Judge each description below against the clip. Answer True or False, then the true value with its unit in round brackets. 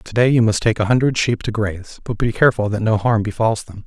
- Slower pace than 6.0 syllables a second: False (6.1 syllables/s)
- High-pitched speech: False (110 Hz)